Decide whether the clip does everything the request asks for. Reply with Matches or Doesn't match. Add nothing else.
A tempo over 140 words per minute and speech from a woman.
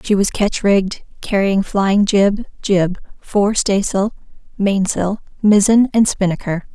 Doesn't match